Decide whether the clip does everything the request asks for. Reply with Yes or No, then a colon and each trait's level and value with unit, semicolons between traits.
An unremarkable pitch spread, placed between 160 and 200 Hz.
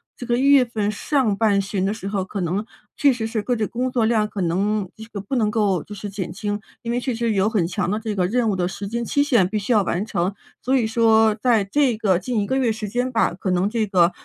No: average, 3.1 semitones; high, 215 Hz